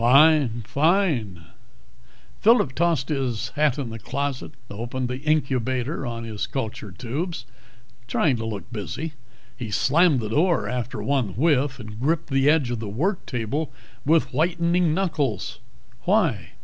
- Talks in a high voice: No, low, 135 Hz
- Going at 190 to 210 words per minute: No, average, 140 wpm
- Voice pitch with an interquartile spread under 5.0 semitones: No, average, 5.3 semitones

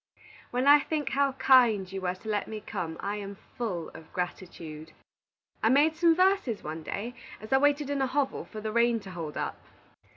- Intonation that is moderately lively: No, wide, 6.8 semitones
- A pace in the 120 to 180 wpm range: No, average, 200 wpm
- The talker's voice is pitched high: Yes, high, 220 Hz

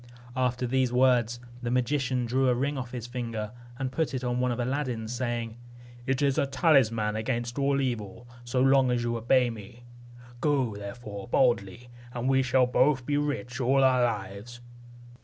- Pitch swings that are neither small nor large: No, narrow, 2.0 semitones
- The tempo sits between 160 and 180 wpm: Yes, average, 175 wpm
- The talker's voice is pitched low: Yes, low, 125 Hz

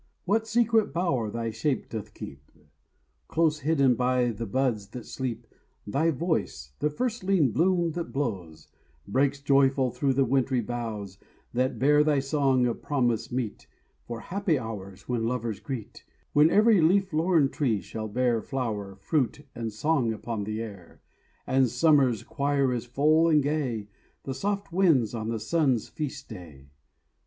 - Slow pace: No, average, 150 wpm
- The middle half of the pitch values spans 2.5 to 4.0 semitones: No, average, 5.2 semitones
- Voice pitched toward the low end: Yes, low, 130 Hz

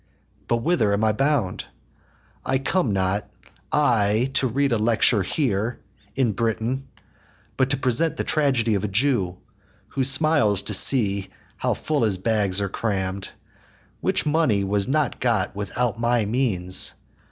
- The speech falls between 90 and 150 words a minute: Yes, average, 145 wpm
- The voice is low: Yes, low, 115 Hz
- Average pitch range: Yes, average, 4.9 semitones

